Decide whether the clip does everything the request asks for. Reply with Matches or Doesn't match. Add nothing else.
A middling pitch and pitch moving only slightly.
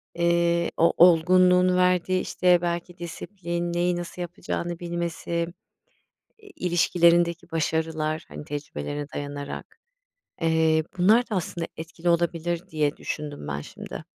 Matches